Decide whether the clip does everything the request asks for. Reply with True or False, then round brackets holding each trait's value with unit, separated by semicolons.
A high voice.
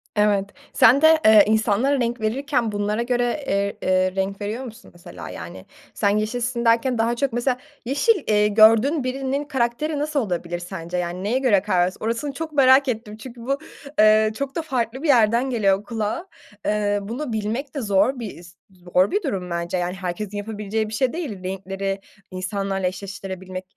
True (215 Hz)